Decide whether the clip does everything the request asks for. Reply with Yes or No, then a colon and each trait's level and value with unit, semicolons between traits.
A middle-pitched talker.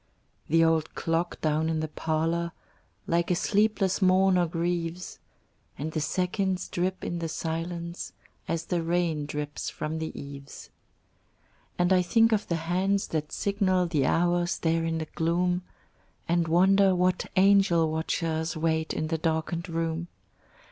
Yes: medium, 170 Hz